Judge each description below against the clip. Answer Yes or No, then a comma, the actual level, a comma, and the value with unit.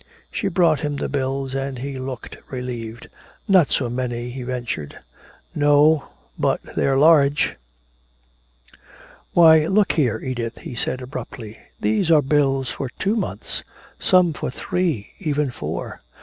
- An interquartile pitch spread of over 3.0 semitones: Yes, average, 3.7 semitones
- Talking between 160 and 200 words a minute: No, slow, 135 wpm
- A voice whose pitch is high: No, low, 135 Hz